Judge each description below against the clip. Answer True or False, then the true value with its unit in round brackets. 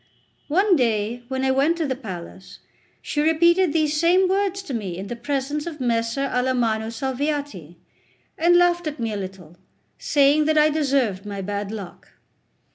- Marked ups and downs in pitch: True (6.0 semitones)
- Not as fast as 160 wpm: False (165 wpm)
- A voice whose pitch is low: False (270 Hz)